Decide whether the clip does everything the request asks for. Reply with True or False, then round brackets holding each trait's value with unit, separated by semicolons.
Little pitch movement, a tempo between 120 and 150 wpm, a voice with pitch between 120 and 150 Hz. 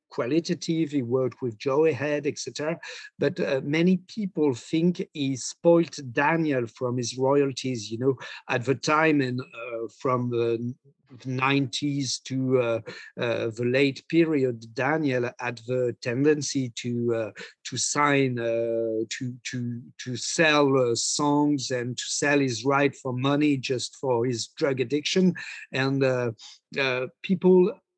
False (3.0 semitones; 140 wpm; 135 Hz)